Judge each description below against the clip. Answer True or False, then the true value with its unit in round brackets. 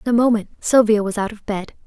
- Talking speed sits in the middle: False (255 wpm)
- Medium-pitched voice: False (215 Hz)